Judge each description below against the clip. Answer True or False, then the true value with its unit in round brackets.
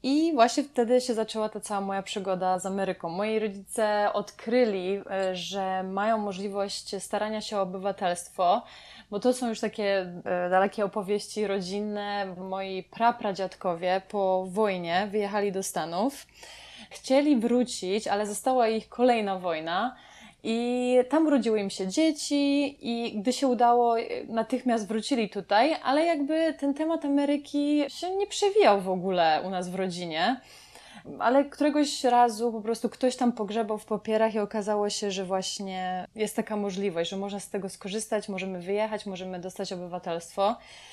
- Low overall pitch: False (210 Hz)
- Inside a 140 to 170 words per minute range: True (145 wpm)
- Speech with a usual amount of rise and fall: True (4.0 semitones)